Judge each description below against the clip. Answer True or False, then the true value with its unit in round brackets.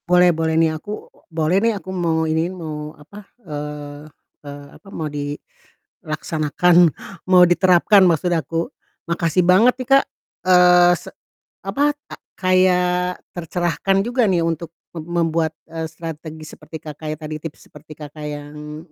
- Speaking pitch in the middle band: True (165 Hz)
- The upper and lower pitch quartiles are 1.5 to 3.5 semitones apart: True (2.7 semitones)